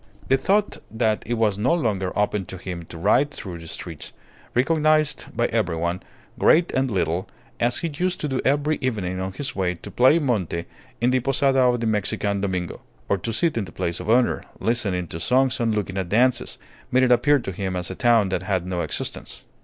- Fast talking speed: Yes, fast, 210 wpm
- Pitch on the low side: Yes, low, 110 Hz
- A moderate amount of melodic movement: No, wide, 5.9 semitones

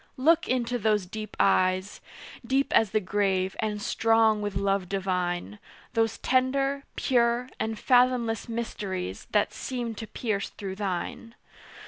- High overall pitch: Yes, high, 220 Hz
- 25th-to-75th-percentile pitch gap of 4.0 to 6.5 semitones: No, average, 3.6 semitones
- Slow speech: Yes, slow, 130 wpm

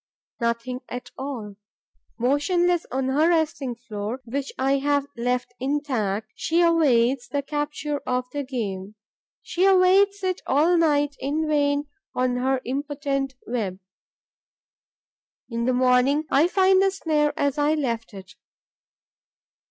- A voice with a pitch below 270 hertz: No, very high, 275 Hz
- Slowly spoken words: Yes, slow, 130 wpm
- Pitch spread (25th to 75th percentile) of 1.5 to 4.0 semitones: Yes, average, 3.5 semitones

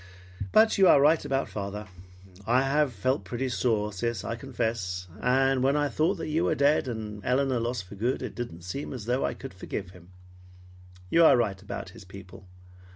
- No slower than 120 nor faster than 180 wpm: No, average, 190 wpm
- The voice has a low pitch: Yes, low, 120 Hz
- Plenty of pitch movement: No, average, 5.0 semitones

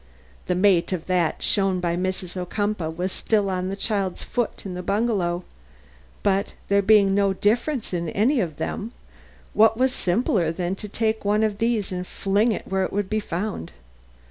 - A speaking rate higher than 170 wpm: Yes, average, 180 wpm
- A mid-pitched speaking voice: No, high, 195 Hz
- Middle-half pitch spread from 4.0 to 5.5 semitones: No, average, 2.9 semitones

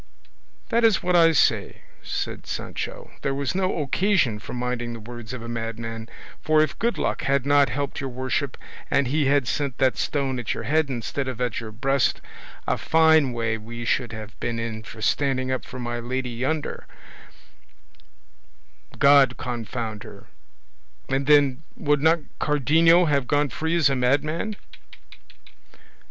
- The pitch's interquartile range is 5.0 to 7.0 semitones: No, average, 3.8 semitones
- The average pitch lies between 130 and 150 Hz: Yes, low, 135 Hz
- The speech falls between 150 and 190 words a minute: Yes, average, 160 wpm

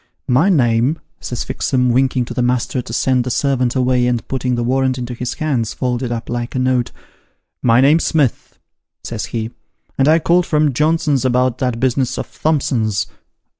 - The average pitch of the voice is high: No, low, 125 Hz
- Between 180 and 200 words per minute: Yes, average, 190 wpm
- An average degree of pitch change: No, narrow, 2.1 semitones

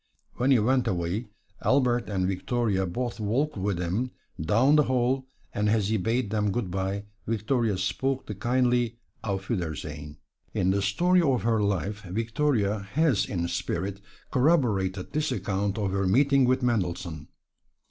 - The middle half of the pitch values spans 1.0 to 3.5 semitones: No, average, 4.7 semitones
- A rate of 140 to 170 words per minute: Yes, average, 150 wpm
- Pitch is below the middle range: Yes, low, 110 Hz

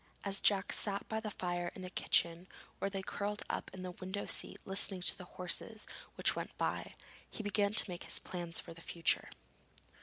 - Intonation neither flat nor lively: No, narrow, 2.3 semitones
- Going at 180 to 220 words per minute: Yes, average, 195 wpm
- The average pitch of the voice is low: No, high, 190 Hz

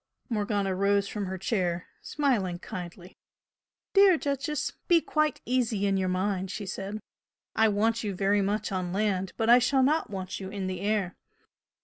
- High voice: Yes, high, 200 Hz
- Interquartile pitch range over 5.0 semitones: No, average, 3.4 semitones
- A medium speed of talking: Yes, average, 165 wpm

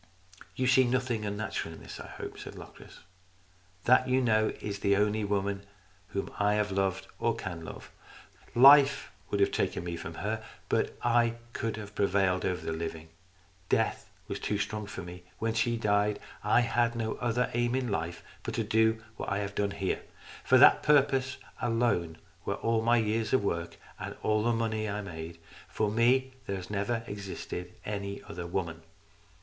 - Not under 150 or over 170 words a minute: No, average, 185 wpm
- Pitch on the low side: Yes, low, 105 Hz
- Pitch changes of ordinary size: Yes, average, 3.3 semitones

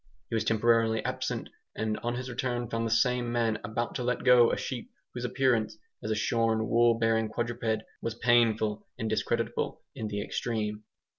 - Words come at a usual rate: Yes, average, 175 wpm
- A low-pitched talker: Yes, low, 115 Hz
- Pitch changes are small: Yes, narrow, 1.6 semitones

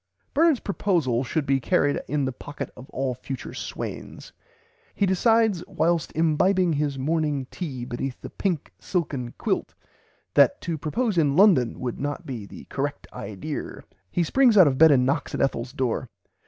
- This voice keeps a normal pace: Yes, average, 165 wpm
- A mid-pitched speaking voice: Yes, medium, 150 Hz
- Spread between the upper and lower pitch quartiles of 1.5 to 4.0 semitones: No, average, 5.3 semitones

